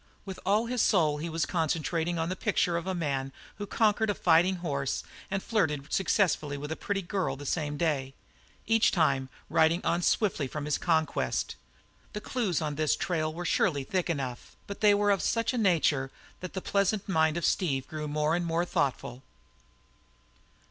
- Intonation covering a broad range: No, average, 4.4 semitones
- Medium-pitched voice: Yes, medium, 170 Hz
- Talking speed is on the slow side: No, average, 185 wpm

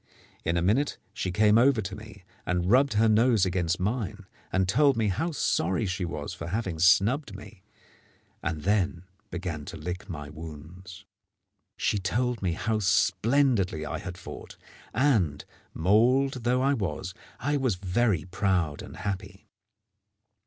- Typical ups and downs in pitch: Yes, average, 4.7 semitones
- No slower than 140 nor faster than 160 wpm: Yes, average, 150 wpm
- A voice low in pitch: Yes, very low, 95 Hz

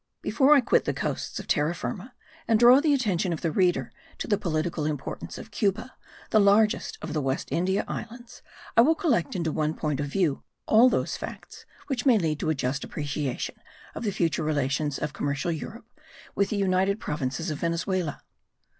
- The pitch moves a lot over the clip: Yes, wide, 6.4 semitones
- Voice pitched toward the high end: No, medium, 175 Hz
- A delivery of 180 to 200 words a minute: Yes, average, 190 wpm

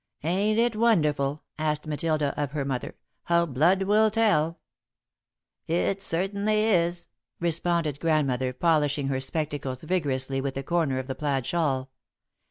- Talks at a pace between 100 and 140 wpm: Yes, slow, 135 wpm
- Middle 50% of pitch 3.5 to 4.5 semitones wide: Yes, average, 4.2 semitones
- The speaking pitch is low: No, medium, 155 Hz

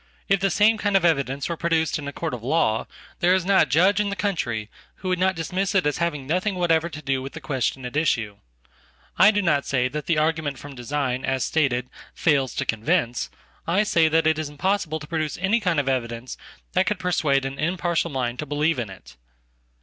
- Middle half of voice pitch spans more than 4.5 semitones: Yes, average, 5.0 semitones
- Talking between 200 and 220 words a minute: Yes, fast, 205 wpm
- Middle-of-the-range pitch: Yes, medium, 155 Hz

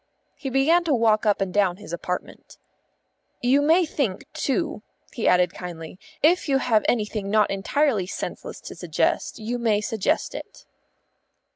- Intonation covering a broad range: Yes, wide, 6.0 semitones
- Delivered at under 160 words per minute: Yes, average, 150 wpm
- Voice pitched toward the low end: No, high, 220 Hz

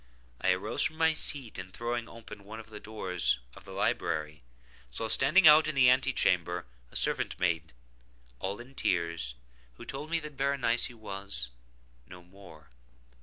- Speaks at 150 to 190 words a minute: Yes, average, 160 wpm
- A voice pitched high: No, low, 105 Hz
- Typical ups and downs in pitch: No, wide, 7.3 semitones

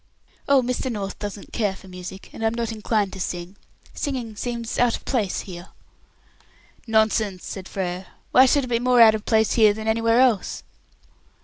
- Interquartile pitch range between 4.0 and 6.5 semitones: No, average, 3.4 semitones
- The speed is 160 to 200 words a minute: Yes, average, 180 wpm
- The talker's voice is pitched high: Yes, high, 220 Hz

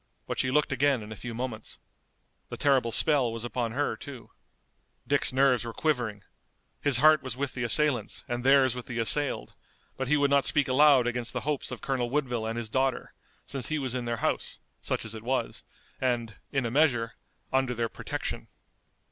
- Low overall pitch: Yes, low, 130 Hz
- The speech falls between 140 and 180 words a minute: No, average, 195 wpm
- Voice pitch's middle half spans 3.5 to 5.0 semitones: No, average, 2.8 semitones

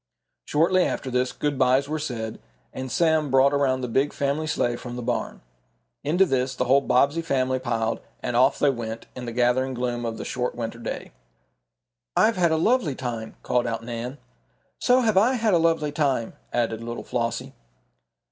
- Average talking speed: Yes, average, 185 wpm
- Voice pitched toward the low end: Yes, low, 130 Hz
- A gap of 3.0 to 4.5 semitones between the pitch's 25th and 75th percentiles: Yes, average, 4.0 semitones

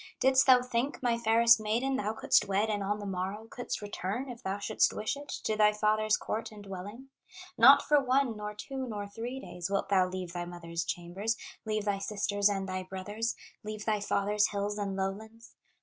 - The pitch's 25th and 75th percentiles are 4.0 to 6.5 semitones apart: No, average, 2.8 semitones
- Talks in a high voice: Yes, high, 210 Hz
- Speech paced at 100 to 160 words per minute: No, average, 195 wpm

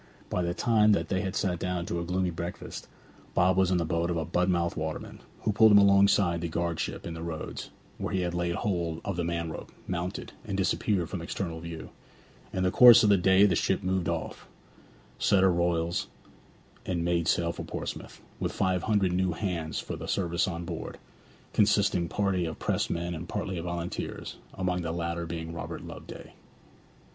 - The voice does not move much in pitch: Yes, narrow, 2.1 semitones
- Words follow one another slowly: No, average, 190 wpm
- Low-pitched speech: Yes, very low, 90 Hz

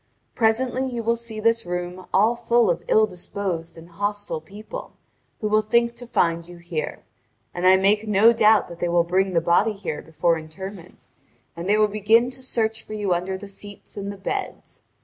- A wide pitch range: No, average, 4.0 semitones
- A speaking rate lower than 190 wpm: No, average, 195 wpm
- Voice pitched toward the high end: Yes, high, 200 Hz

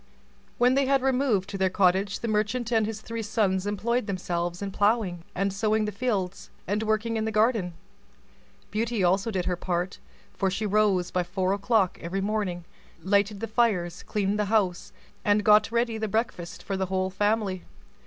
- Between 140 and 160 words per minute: No, average, 180 wpm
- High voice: Yes, high, 205 Hz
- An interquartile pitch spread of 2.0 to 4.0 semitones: Yes, average, 2.9 semitones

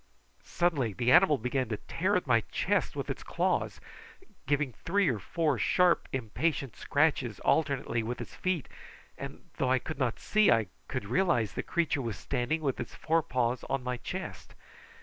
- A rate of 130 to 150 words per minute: No, average, 170 wpm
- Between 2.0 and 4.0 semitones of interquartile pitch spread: No, average, 5.1 semitones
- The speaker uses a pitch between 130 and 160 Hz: Yes, low, 135 Hz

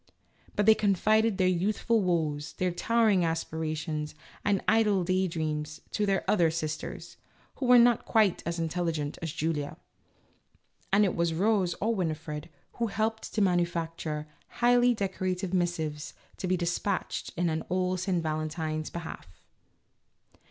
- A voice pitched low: No, medium, 175 Hz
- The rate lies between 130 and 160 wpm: Yes, average, 140 wpm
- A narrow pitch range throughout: No, average, 4.2 semitones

